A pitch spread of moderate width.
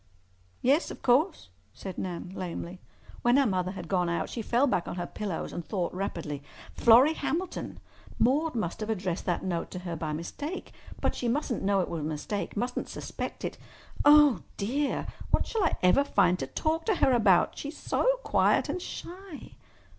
No: wide, 8.1 semitones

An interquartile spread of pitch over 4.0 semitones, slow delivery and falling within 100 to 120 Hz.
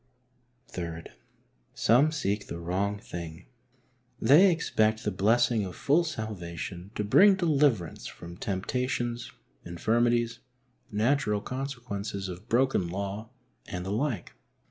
Yes: average, 5.2 semitones; slow, 110 wpm; low, 110 Hz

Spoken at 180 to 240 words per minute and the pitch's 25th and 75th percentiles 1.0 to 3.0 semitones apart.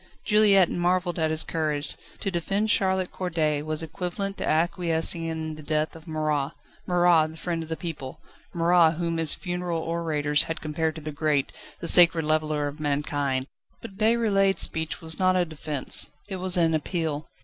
No: average, 170 wpm; narrow, 2.5 semitones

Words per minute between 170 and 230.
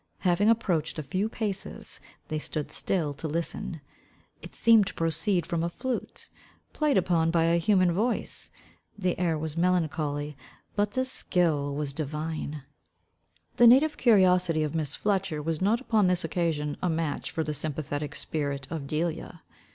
No: average, 155 wpm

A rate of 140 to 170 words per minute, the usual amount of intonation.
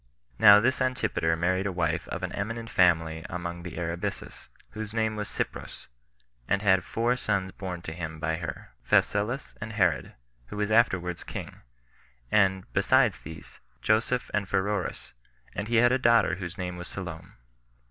Yes: average, 160 wpm; average, 4.0 semitones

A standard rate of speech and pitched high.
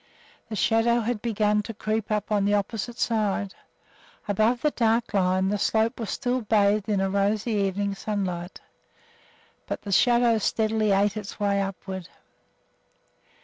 Yes: average, 150 wpm; high, 210 Hz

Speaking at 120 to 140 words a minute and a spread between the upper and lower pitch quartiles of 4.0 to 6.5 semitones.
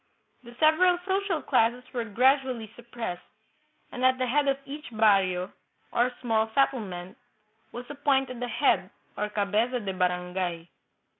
Yes: slow, 135 wpm; average, 4.7 semitones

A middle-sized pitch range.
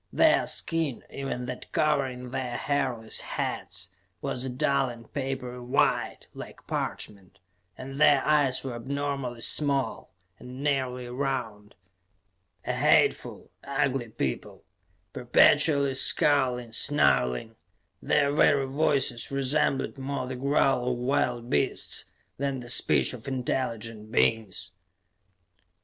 No: narrow, 2.3 semitones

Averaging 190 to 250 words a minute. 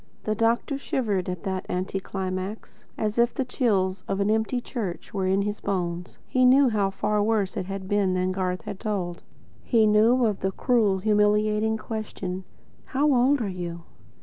No: average, 175 wpm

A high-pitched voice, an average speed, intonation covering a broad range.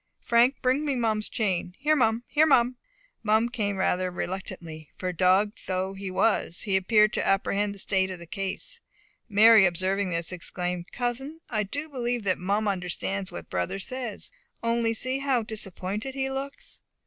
No: high, 210 Hz; average, 165 wpm; average, 4.6 semitones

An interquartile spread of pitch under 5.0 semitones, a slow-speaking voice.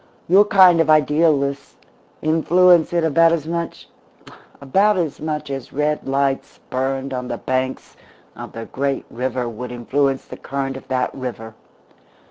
No: average, 3.8 semitones; average, 145 wpm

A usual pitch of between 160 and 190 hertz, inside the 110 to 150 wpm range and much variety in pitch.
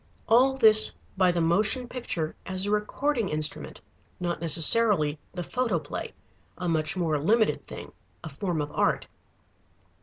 Yes: medium, 185 Hz; average, 140 wpm; wide, 5.7 semitones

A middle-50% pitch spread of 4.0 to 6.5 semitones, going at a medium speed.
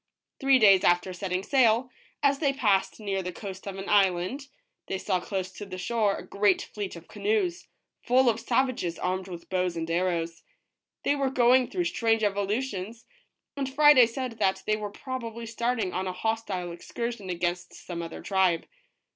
Yes: average, 5.0 semitones; average, 175 wpm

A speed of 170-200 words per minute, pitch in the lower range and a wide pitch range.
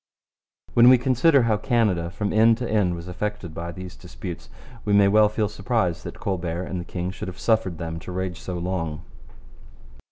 No: average, 190 wpm; very low, 95 Hz; average, 4.0 semitones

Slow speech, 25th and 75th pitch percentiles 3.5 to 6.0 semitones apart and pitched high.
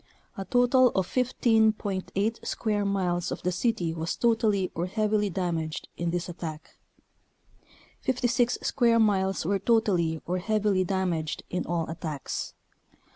Yes: slow, 130 wpm; average, 4.2 semitones; high, 195 Hz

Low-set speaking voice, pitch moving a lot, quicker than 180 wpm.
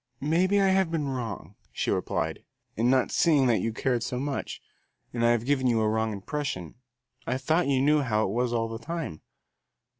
No: low, 125 Hz; average, 4.4 semitones; average, 190 wpm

